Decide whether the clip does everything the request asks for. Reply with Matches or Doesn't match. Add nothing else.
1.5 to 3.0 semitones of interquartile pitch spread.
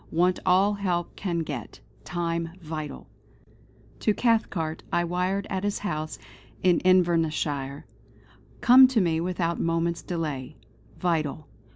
Matches